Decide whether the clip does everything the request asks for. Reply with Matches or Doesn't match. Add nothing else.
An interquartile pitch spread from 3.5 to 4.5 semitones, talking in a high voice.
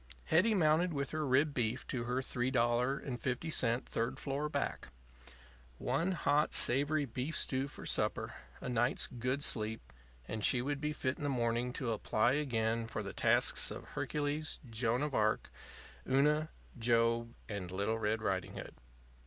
Doesn't match